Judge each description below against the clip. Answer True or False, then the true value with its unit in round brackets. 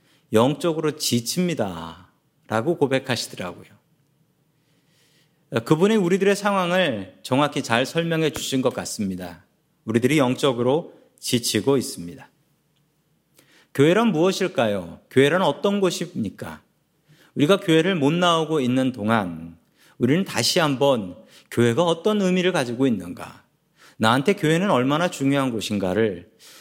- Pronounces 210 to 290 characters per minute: True (280 characters per minute)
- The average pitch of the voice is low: False (145 Hz)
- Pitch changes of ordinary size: False (6.3 semitones)